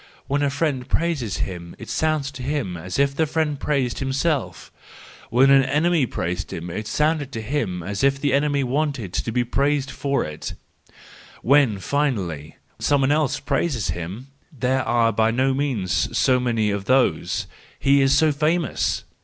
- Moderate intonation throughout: Yes, average, 4.3 semitones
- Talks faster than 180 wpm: No, average, 165 wpm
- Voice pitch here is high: No, low, 135 Hz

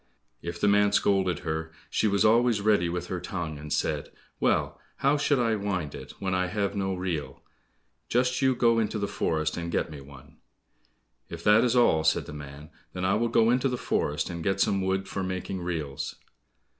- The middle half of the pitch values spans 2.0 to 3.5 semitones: No, average, 4.7 semitones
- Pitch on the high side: No, very low, 95 Hz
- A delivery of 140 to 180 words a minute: No, average, 200 wpm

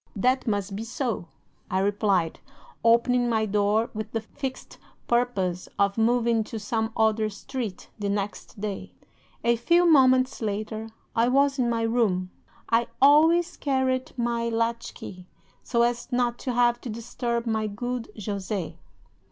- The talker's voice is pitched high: Yes, high, 230 Hz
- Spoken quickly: No, average, 145 wpm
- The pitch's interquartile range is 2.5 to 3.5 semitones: Yes, average, 2.8 semitones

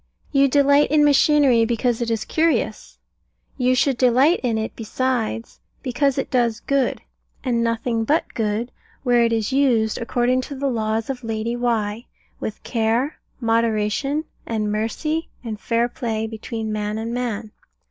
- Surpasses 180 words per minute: No, average, 150 wpm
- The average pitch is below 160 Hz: No, high, 235 Hz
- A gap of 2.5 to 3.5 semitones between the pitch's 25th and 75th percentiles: Yes, average, 3.0 semitones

